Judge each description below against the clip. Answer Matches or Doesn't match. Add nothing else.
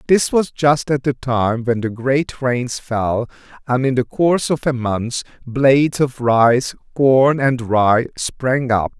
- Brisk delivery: Doesn't match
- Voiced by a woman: Doesn't match